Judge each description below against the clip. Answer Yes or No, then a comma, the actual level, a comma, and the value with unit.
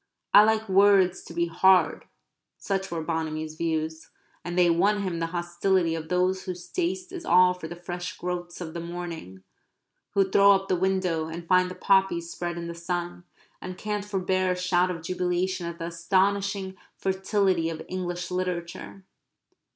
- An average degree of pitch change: No, narrow, 2.0 semitones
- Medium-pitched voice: Yes, medium, 180 Hz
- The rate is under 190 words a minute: Yes, average, 170 wpm